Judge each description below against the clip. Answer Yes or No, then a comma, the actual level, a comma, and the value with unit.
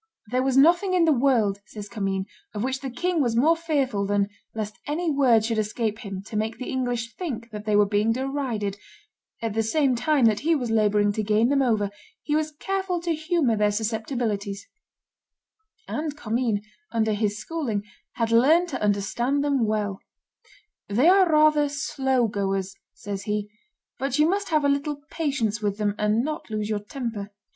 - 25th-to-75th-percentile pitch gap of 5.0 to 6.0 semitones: Yes, wide, 5.5 semitones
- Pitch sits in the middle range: No, high, 235 Hz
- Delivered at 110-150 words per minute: No, average, 180 wpm